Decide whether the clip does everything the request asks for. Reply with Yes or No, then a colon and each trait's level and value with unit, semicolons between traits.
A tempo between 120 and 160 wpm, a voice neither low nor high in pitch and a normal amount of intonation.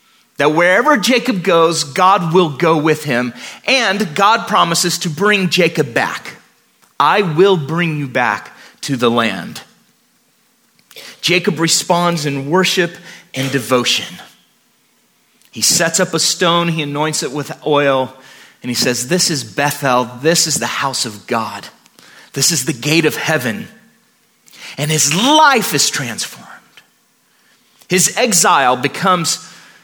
Yes: slow, 135 wpm; medium, 165 Hz; average, 4.4 semitones